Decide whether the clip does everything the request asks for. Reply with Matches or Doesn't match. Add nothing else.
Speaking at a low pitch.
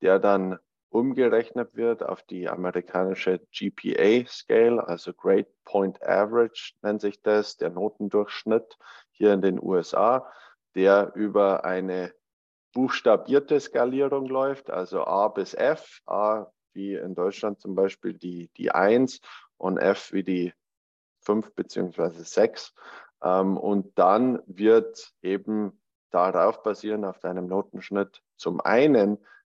Matches